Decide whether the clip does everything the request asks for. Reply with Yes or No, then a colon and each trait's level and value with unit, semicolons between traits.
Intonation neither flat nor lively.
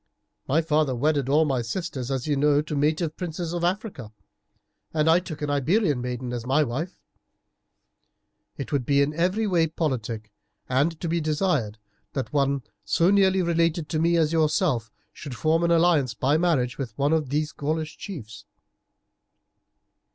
Yes: average, 3.9 semitones